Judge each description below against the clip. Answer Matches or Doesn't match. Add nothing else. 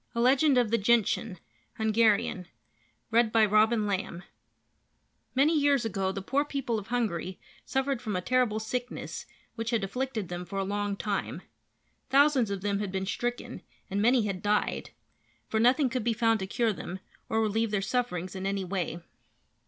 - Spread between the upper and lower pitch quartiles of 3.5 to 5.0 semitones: Matches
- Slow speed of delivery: Doesn't match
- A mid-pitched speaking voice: Doesn't match